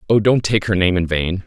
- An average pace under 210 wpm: No, fast, 285 wpm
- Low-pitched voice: Yes, very low, 95 Hz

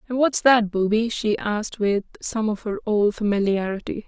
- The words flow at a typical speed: Yes, average, 175 wpm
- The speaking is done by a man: No, female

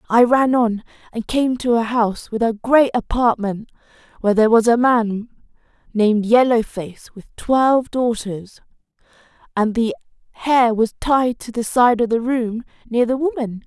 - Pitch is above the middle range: Yes, high, 235 Hz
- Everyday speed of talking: Yes, average, 160 wpm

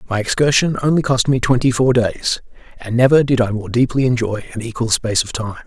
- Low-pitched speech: Yes, low, 120 Hz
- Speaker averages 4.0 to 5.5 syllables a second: No, 5.8 syllables/s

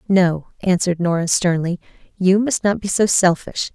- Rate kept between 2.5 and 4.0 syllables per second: No, 4.8 syllables/s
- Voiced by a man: No, female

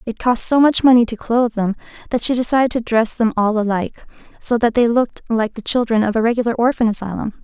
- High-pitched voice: Yes, high, 230 Hz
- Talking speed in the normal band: No, fast, 225 wpm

